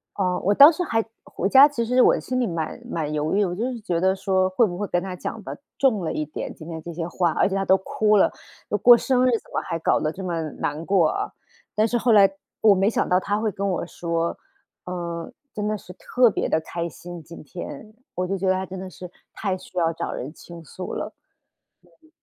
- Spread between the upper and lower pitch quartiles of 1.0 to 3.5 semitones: No, average, 3.9 semitones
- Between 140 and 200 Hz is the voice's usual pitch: Yes, high, 190 Hz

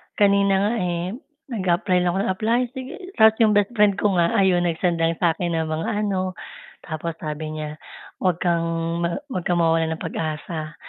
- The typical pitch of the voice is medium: Yes, medium, 175 Hz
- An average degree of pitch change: Yes, average, 3.3 semitones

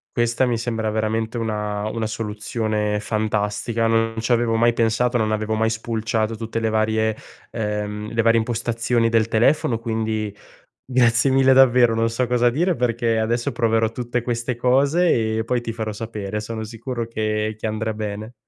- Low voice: Yes, low, 115 Hz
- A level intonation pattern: Yes, narrow, 1.5 semitones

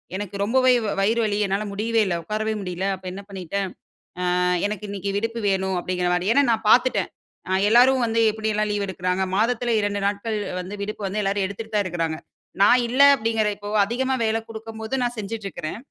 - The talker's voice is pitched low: No, high, 210 Hz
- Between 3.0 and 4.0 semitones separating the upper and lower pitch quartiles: No, narrow, 2.6 semitones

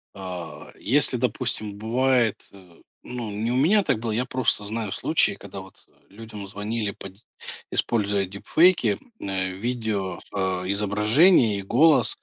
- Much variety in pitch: No, average, 3.8 semitones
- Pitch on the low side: Yes, low, 110 Hz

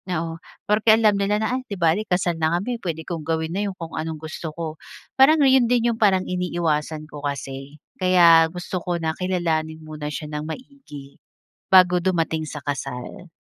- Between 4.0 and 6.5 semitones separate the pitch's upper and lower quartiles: No, average, 3.2 semitones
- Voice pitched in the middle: Yes, medium, 170 Hz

